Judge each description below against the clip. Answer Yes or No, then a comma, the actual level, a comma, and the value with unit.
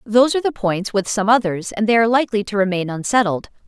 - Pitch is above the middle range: Yes, high, 215 Hz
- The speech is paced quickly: No, average, 195 wpm